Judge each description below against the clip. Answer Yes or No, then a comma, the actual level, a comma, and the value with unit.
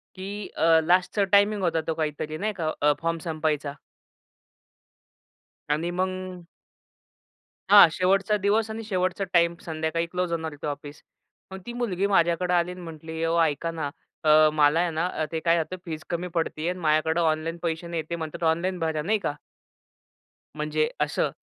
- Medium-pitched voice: Yes, medium, 165 Hz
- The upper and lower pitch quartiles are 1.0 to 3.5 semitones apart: Yes, average, 2.7 semitones